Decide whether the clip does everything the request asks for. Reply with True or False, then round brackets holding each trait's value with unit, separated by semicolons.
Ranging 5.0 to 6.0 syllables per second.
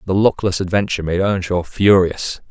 True (5.2 syllables/s)